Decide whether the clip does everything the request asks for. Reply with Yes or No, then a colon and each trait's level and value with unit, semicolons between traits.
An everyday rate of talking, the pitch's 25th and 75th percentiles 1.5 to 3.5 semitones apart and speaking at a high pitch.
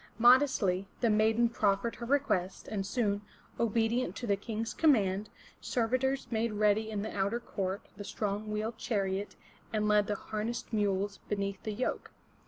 Yes: average, 155 wpm; narrow, 2.6 semitones; high, 215 Hz